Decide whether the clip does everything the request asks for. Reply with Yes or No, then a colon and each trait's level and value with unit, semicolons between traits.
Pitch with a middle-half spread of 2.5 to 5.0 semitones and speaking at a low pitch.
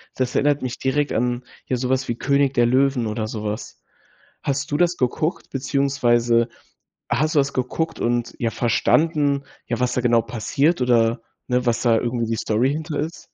Yes: average, 2.9 semitones; low, 125 Hz